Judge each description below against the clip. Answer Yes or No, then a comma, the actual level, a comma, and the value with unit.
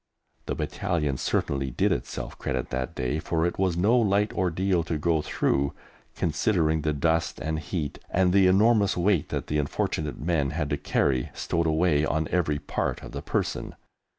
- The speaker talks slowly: No, average, 175 wpm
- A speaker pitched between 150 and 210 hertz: No, very low, 80 Hz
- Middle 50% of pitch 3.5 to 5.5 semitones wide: Yes, average, 3.9 semitones